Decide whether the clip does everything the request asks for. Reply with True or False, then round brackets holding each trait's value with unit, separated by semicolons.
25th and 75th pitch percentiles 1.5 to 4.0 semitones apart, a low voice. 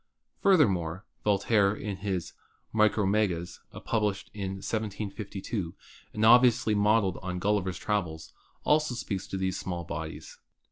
True (2.5 semitones; 100 Hz)